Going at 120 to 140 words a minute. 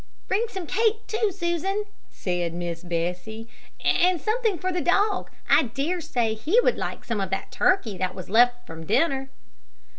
No: average, 170 wpm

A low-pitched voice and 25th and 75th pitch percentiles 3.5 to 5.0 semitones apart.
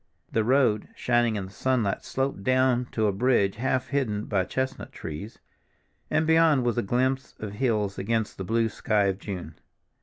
Yes: low, 115 Hz; average, 4.2 semitones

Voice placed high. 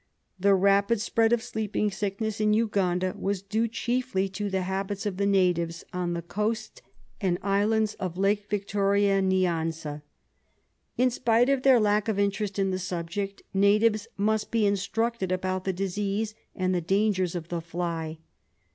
Yes: high, 200 Hz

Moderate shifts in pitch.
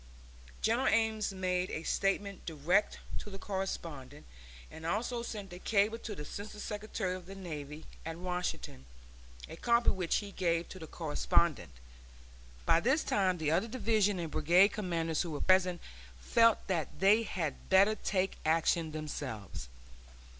Yes: average, 4.3 semitones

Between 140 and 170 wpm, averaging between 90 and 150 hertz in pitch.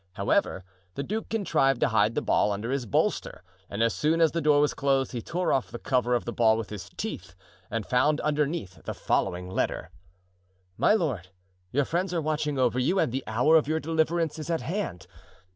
No: average, 200 wpm; low, 135 Hz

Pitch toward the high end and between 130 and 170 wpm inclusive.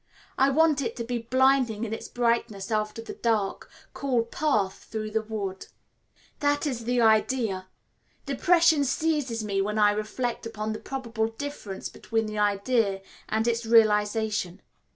Yes: high, 225 Hz; average, 150 wpm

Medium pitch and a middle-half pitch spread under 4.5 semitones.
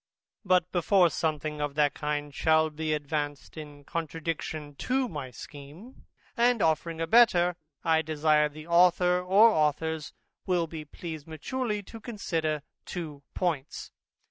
Yes: medium, 160 Hz; average, 3.1 semitones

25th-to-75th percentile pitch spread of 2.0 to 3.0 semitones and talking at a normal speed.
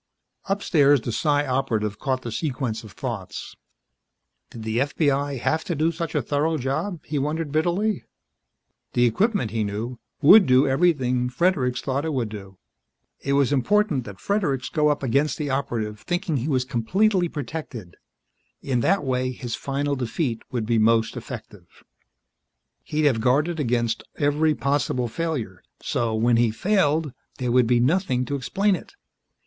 No: average, 4.6 semitones; average, 155 wpm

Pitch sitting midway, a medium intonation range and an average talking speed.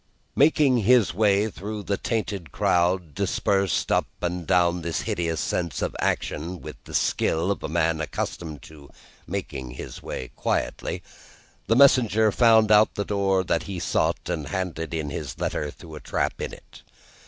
No: very low, 95 Hz; average, 4.3 semitones; average, 160 wpm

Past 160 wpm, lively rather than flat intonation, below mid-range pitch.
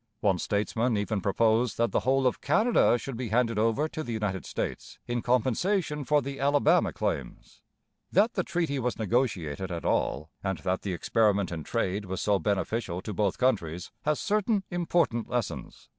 Yes: average, 175 wpm; wide, 5.7 semitones; low, 115 Hz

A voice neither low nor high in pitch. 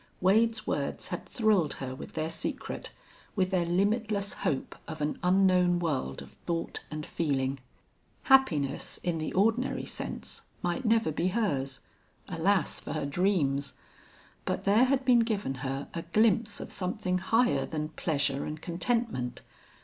Yes: medium, 175 Hz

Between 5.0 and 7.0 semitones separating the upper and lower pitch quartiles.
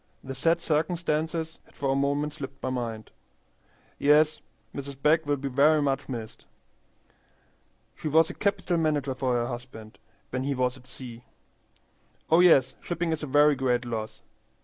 No: average, 3.4 semitones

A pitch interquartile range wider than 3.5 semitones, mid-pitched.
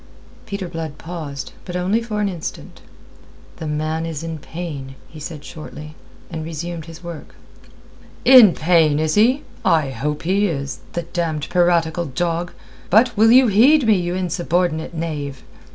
No: average, 2.8 semitones; medium, 170 Hz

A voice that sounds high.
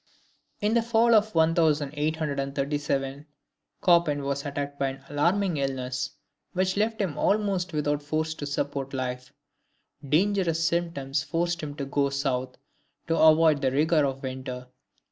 No: medium, 150 Hz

